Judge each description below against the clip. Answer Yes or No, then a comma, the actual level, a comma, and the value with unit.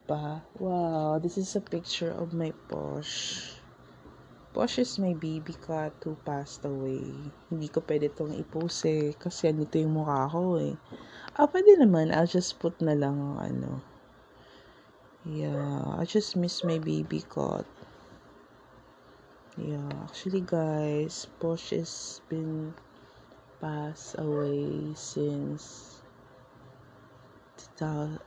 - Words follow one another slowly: Yes, slow, 115 wpm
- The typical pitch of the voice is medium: Yes, medium, 155 Hz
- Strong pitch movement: No, average, 4.0 semitones